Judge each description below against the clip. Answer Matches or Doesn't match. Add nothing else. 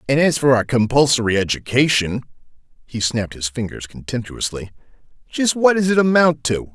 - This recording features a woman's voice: Doesn't match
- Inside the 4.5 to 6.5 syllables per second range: Matches